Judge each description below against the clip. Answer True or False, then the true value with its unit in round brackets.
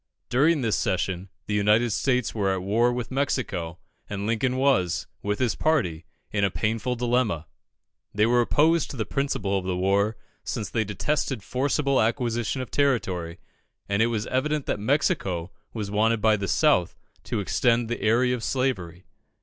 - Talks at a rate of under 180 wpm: True (165 wpm)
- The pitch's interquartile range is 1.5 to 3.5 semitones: False (4.4 semitones)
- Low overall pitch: True (115 Hz)